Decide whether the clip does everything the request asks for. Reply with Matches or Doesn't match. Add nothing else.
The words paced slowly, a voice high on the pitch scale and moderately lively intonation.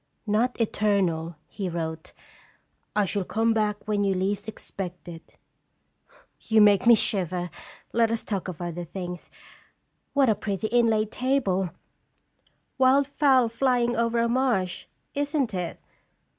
Matches